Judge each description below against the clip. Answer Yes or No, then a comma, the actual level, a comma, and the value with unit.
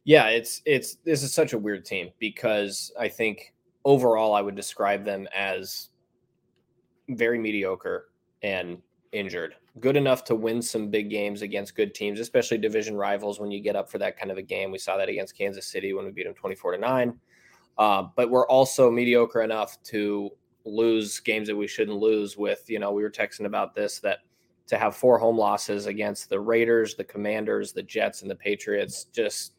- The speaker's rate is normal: Yes, average, 195 wpm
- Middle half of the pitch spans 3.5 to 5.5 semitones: No, average, 2.8 semitones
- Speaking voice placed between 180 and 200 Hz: No, low, 110 Hz